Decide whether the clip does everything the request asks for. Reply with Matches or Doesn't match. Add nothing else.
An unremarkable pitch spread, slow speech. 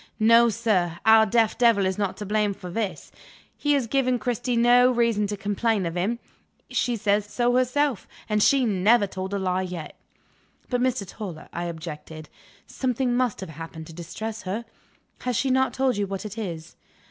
Doesn't match